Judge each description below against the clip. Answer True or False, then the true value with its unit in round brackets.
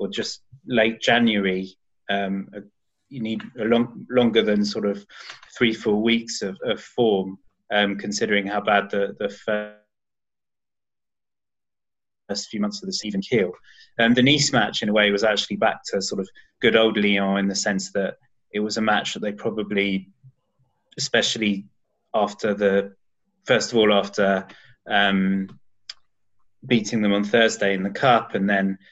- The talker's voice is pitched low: True (105 Hz)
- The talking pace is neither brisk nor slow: True (160 wpm)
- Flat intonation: True (2.2 semitones)